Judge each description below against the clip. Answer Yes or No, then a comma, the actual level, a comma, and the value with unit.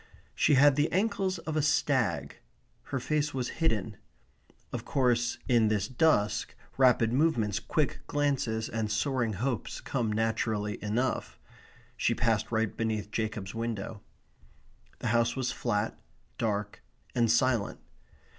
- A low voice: Yes, low, 115 Hz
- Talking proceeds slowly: Yes, slow, 125 wpm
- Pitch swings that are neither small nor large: Yes, average, 3.8 semitones